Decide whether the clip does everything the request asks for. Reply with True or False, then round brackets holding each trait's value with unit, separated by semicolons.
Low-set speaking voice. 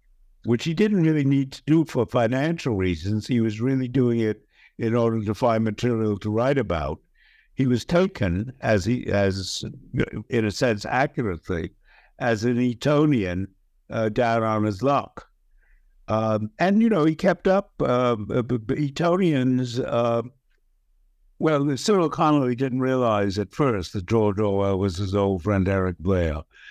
True (115 Hz)